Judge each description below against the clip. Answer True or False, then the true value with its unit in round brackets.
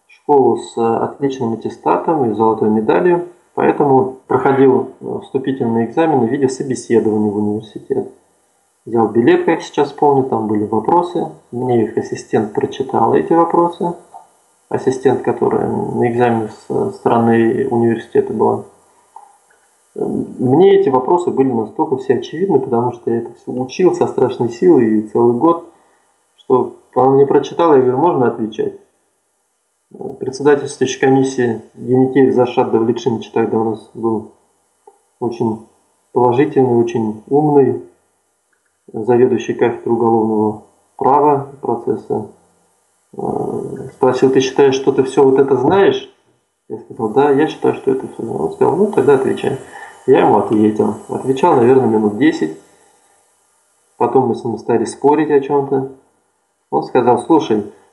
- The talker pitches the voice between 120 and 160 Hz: True (135 Hz)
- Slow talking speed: False (130 wpm)